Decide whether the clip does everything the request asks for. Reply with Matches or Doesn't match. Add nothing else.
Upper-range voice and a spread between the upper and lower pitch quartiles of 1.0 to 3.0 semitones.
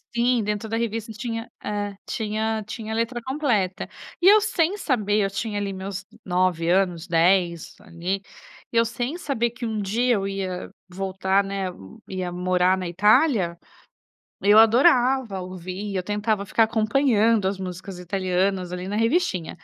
Doesn't match